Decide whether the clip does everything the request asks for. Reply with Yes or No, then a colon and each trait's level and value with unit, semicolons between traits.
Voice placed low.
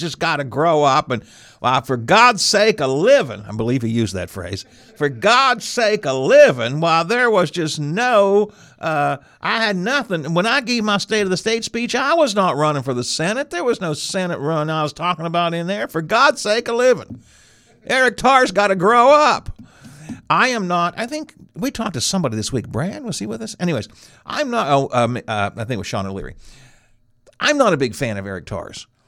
No: medium, 170 Hz